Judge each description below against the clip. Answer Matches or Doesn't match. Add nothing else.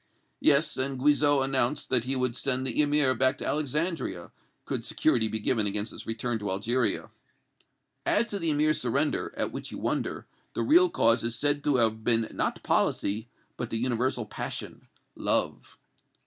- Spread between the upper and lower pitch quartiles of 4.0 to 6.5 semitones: Matches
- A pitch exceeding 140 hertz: Doesn't match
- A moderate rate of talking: Matches